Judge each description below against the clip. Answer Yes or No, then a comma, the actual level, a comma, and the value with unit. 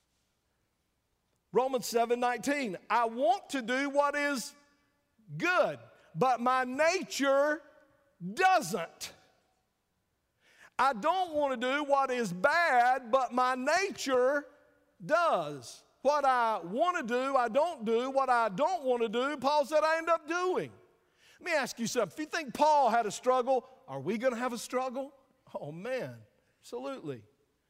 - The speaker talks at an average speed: Yes, average, 145 wpm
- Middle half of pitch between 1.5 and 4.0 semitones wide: Yes, average, 3.5 semitones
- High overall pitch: Yes, very high, 265 Hz